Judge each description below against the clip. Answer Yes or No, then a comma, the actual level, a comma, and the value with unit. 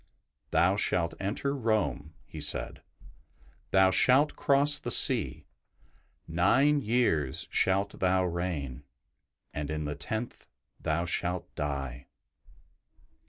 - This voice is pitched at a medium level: No, very low, 90 Hz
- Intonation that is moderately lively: No, wide, 6.2 semitones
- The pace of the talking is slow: Yes, slow, 110 wpm